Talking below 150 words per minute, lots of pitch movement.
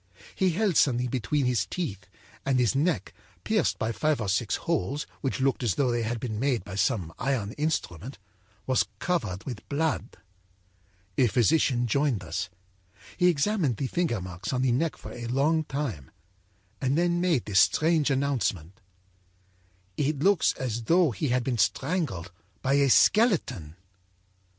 No: average, 155 wpm; wide, 5.8 semitones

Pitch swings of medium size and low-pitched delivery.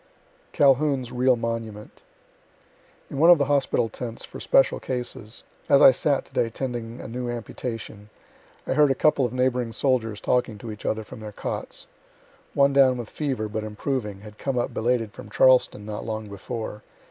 Yes: average, 3.2 semitones; low, 120 Hz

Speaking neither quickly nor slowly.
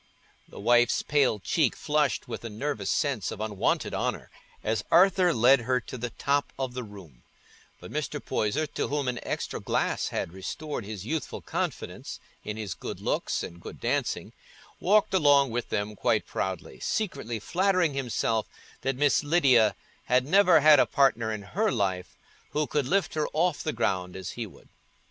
Yes: average, 170 wpm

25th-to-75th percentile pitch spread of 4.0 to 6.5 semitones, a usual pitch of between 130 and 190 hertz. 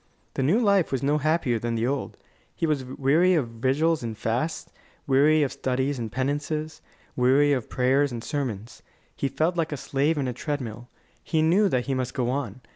No: average, 3.6 semitones; medium, 140 Hz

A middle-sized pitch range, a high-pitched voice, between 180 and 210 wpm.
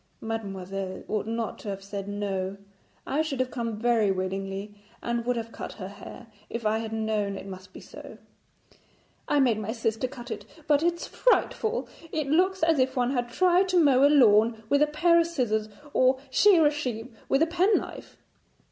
No: wide, 6.0 semitones; high, 235 Hz; average, 190 wpm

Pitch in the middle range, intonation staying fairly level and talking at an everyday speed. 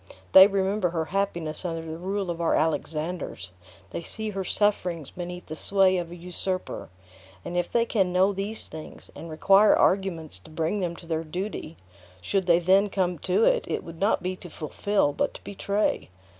No: medium, 180 Hz; average, 3.1 semitones; average, 185 wpm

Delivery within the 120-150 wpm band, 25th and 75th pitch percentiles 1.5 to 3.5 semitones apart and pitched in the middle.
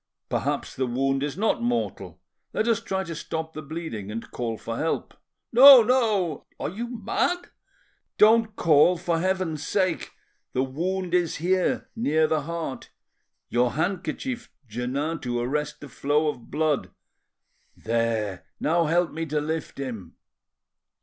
No: average, 140 wpm; wide, 5.6 semitones; medium, 160 Hz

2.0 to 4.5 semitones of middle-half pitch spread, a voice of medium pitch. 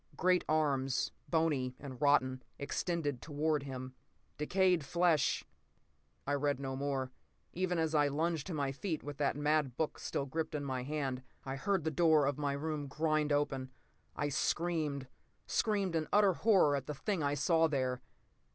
Yes: average, 2.8 semitones; medium, 145 Hz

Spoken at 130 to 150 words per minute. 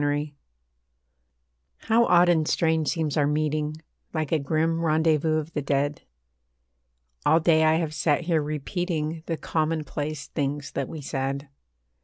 Yes: average, 140 wpm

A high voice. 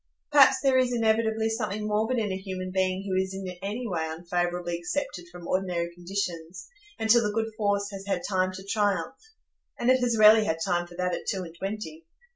Yes: high, 195 Hz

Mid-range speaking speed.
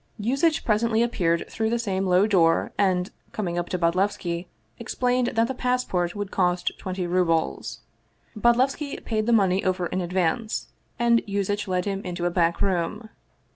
Yes: average, 160 wpm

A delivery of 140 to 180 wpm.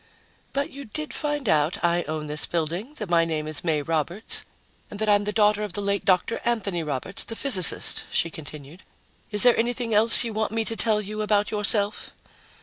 No: average, 200 wpm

